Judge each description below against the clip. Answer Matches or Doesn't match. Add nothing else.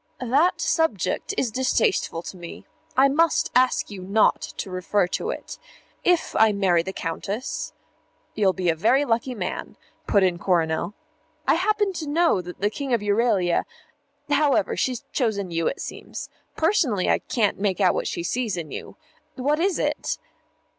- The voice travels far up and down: Matches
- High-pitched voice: Matches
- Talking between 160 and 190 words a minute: Matches